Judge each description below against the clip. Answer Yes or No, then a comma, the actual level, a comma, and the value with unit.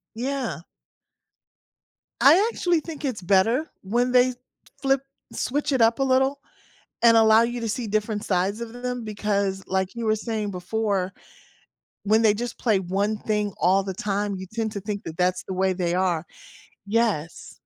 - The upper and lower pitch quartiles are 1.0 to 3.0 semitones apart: No, average, 4.0 semitones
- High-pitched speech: Yes, high, 215 Hz